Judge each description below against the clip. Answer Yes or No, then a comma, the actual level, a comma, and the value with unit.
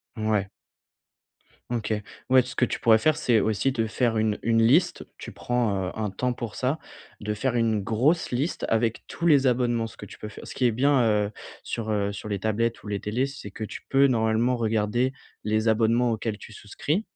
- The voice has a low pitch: Yes, low, 115 Hz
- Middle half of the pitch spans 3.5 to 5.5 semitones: No, average, 2.7 semitones